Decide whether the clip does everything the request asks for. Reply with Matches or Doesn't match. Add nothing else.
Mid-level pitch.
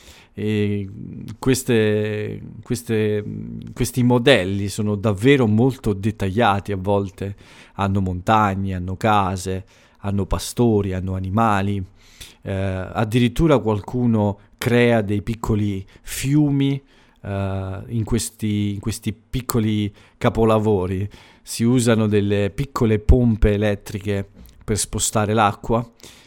Doesn't match